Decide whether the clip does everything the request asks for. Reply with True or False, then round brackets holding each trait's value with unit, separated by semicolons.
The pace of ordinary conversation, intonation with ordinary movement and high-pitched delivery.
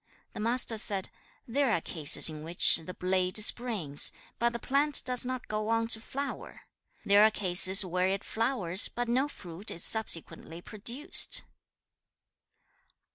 True (145 wpm; 4.9 semitones; 215 Hz)